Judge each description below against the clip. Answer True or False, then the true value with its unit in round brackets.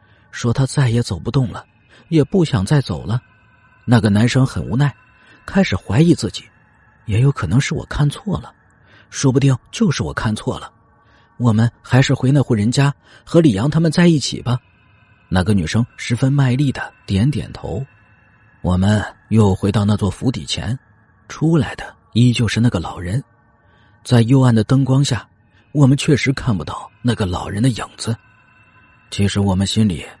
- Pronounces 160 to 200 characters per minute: False (240 characters per minute)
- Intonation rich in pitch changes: False (4.4 semitones)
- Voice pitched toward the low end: True (115 Hz)